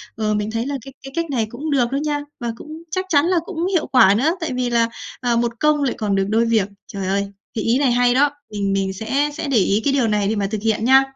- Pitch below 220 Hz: No, high, 240 Hz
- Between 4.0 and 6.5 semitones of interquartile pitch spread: Yes, average, 5.0 semitones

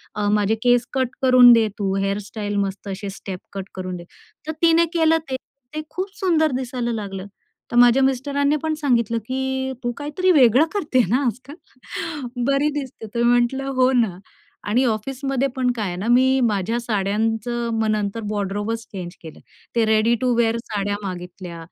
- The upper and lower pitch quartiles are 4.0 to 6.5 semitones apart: Yes, average, 4.4 semitones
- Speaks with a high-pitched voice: Yes, high, 235 Hz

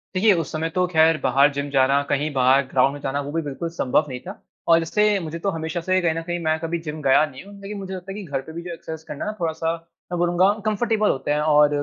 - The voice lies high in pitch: No, medium, 160 Hz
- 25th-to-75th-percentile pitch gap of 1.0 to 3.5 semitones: No, average, 3.9 semitones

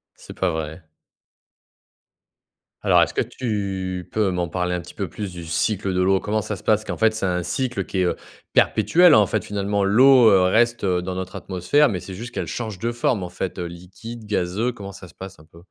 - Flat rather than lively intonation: No, average, 3.5 semitones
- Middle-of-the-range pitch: No, very low, 95 Hz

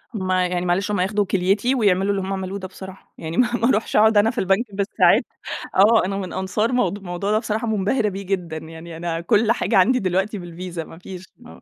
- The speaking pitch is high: Yes, high, 195 Hz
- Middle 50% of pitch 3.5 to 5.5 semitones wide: No, average, 2.8 semitones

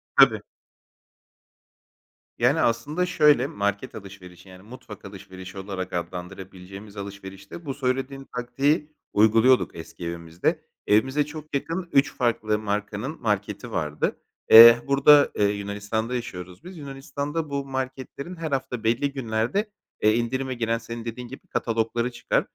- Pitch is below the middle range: Yes, low, 115 Hz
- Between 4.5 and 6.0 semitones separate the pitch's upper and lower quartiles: Yes, average, 5.2 semitones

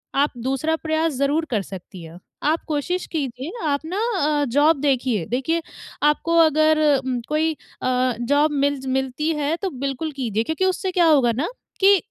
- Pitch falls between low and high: No, very high, 295 Hz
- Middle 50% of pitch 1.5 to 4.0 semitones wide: Yes, average, 3.6 semitones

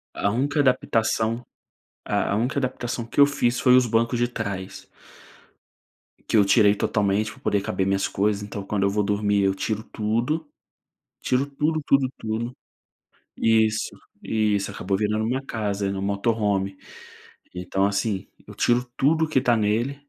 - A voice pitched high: No, low, 110 Hz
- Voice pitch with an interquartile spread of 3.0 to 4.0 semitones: Yes, average, 3.5 semitones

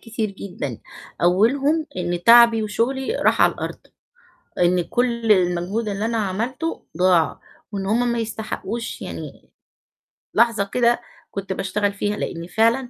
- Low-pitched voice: No, high, 215 Hz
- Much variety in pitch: No, average, 4.0 semitones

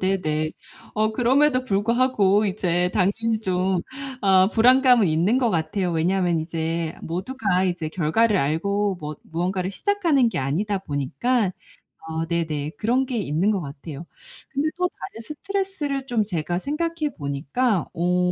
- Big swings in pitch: Yes, wide, 6.3 semitones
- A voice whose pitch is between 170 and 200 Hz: Yes, high, 190 Hz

